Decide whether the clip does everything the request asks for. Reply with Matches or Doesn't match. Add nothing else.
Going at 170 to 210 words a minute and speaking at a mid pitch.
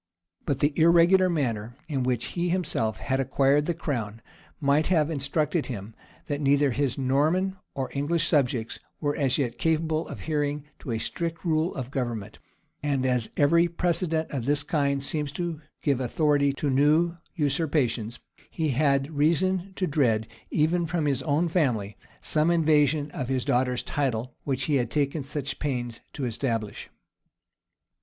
Doesn't match